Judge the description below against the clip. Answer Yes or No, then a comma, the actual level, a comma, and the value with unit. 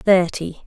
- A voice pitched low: No, medium, 180 Hz